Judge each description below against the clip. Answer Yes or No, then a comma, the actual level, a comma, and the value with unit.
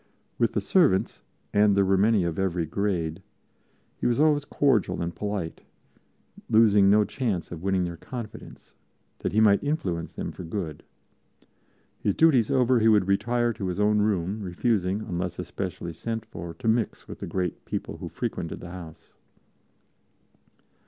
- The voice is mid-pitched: No, low, 100 Hz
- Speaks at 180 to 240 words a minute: No, average, 160 wpm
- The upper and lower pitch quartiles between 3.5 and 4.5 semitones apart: Yes, average, 4.1 semitones